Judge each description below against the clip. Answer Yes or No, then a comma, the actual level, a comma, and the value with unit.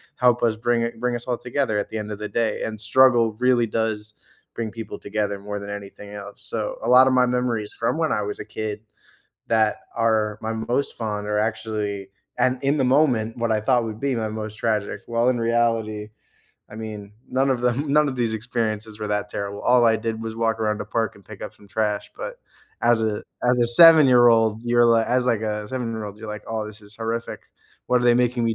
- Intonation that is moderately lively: No, narrow, 2.2 semitones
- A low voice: Yes, low, 115 Hz